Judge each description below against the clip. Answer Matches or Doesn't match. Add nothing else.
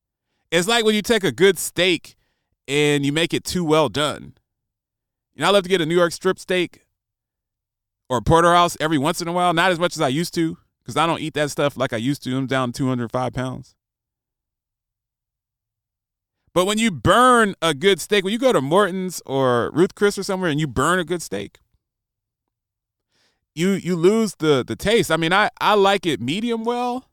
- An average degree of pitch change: Doesn't match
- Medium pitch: Matches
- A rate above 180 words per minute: Matches